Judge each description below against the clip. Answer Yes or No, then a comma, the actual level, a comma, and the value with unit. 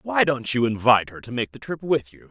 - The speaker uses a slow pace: No, fast, 285 wpm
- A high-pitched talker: No, low, 125 Hz